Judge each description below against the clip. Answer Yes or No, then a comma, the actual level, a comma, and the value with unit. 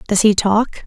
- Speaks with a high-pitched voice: Yes, high, 210 Hz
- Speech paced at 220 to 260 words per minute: No, fast, 210 wpm